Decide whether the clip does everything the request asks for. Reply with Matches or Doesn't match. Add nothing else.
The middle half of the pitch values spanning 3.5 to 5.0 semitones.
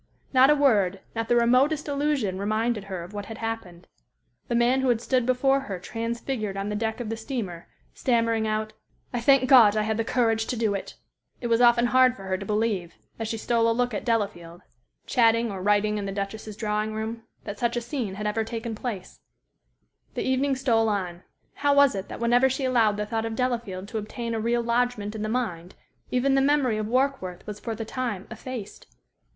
Doesn't match